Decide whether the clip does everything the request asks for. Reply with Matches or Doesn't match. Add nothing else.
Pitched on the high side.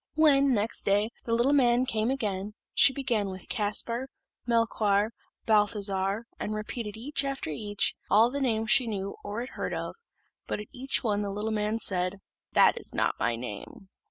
Matches